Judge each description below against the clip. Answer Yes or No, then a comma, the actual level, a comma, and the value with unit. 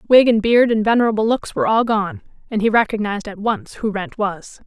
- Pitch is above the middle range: Yes, high, 215 Hz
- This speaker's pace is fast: Yes, fast, 220 wpm